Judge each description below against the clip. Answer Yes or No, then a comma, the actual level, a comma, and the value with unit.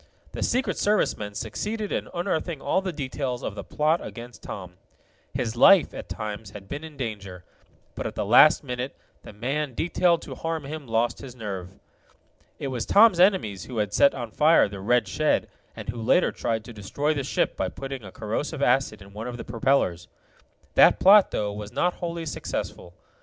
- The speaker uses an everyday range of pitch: No, wide, 6.5 semitones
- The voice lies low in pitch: Yes, low, 125 Hz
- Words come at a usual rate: Yes, average, 190 wpm